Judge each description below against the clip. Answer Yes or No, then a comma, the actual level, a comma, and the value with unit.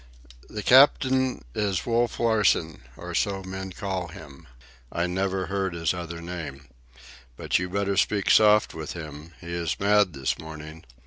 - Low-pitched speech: Yes, very low, 95 Hz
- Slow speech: No, average, 150 wpm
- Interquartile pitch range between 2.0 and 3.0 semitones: No, average, 3.7 semitones